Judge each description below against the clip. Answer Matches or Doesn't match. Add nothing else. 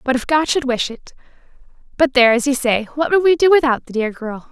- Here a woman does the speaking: Matches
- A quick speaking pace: Matches